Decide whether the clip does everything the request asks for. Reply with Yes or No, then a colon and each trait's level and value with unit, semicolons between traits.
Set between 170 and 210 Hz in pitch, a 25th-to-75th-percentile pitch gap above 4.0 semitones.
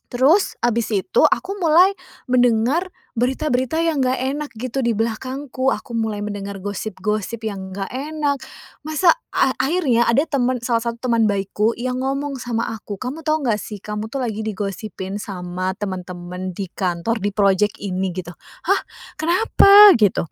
No: high, 230 Hz; average, 5.2 semitones